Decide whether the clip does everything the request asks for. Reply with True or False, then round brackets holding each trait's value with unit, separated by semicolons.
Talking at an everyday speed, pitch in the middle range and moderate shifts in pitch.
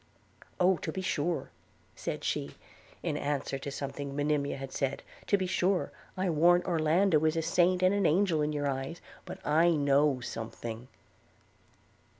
True (160 wpm; 150 Hz; 4.0 semitones)